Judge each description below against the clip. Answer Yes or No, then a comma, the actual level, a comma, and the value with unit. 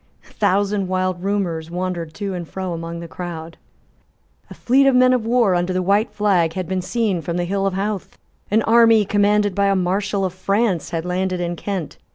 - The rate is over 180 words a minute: Yes, fast, 205 wpm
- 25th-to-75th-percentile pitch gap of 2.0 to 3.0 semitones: Yes, narrow, 2.6 semitones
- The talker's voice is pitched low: No, high, 190 Hz